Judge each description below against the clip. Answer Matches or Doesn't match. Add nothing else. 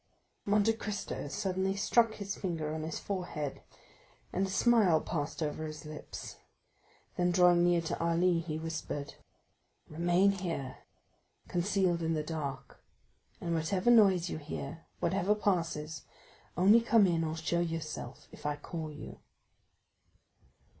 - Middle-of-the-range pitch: Matches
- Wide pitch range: Doesn't match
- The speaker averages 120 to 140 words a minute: Matches